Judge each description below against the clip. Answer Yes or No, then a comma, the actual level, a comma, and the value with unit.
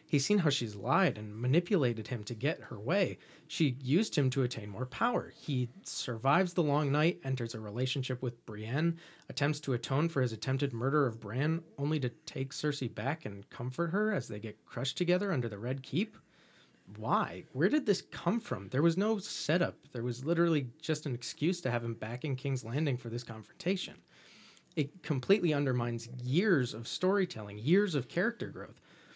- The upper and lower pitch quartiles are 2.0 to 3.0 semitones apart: No, wide, 5.6 semitones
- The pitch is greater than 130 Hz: Yes, medium, 140 Hz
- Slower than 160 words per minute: No, average, 185 wpm